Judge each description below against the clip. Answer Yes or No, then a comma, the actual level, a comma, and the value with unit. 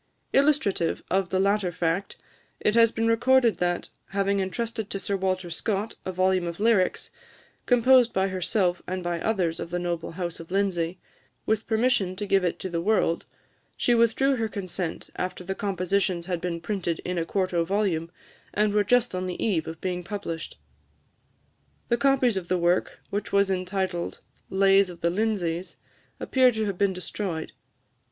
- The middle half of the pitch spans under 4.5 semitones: Yes, average, 3.2 semitones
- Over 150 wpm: Yes, average, 170 wpm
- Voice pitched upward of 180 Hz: Yes, high, 190 Hz